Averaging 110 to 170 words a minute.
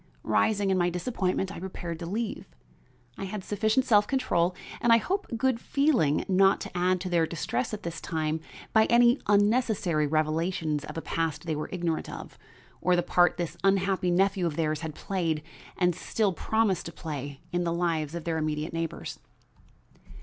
No: average, 180 wpm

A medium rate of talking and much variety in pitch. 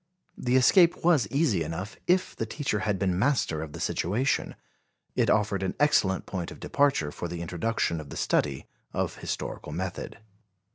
Yes: average, 170 wpm; wide, 7.7 semitones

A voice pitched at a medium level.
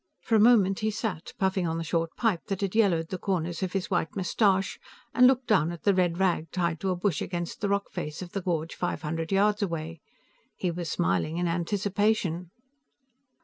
Yes: medium, 180 Hz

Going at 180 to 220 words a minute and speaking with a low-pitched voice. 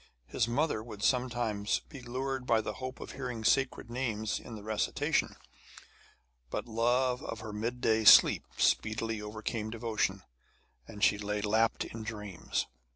No: average, 150 wpm; low, 115 Hz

